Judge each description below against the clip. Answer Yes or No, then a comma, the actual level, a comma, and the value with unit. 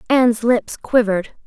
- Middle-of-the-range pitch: No, high, 230 Hz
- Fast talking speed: No, slow, 125 wpm